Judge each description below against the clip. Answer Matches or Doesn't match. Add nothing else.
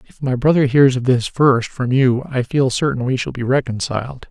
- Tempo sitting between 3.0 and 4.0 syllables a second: Doesn't match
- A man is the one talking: Matches